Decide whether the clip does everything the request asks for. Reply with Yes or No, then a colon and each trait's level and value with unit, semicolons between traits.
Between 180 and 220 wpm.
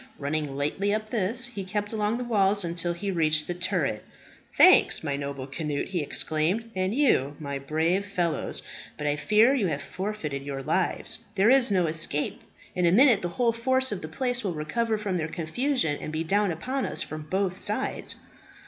Yes: average, 190 wpm